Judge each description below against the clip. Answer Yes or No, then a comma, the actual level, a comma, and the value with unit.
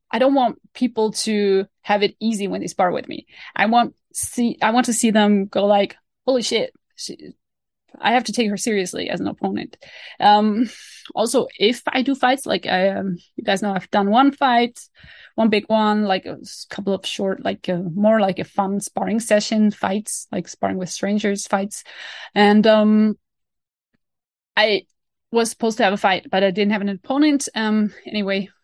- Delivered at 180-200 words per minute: Yes, average, 190 wpm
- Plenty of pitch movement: No, average, 2.9 semitones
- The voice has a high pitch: Yes, high, 215 Hz